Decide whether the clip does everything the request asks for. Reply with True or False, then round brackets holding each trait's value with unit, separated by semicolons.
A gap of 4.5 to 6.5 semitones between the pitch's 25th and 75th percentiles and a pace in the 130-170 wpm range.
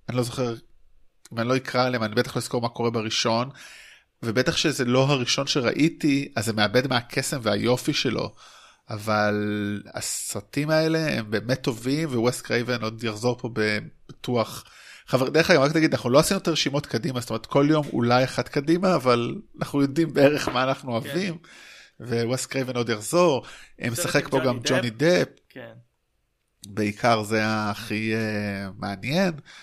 False (3.9 semitones; 150 wpm)